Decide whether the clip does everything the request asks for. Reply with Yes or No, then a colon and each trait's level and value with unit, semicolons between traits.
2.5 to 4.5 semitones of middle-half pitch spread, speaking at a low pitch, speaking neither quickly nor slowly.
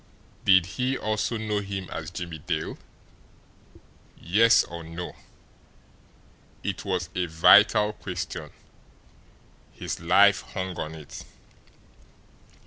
No: average, 3.7 semitones; very low, 90 Hz; slow, 100 wpm